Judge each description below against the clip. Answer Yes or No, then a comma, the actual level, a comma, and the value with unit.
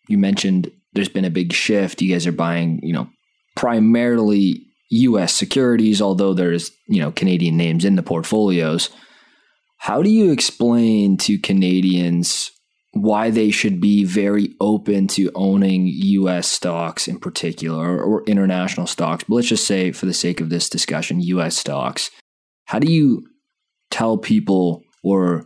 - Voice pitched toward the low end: Yes, low, 100 Hz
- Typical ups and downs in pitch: Yes, average, 4.0 semitones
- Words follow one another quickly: No, average, 155 wpm